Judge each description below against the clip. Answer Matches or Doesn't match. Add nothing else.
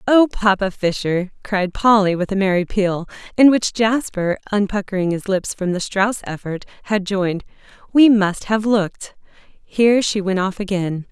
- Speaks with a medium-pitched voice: Doesn't match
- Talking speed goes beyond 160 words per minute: Doesn't match